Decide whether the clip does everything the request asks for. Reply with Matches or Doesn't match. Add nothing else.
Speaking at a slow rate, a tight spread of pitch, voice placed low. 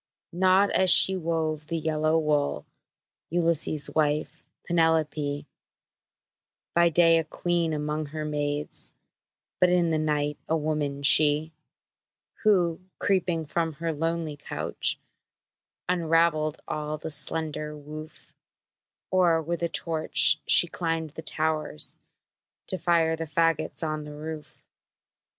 Doesn't match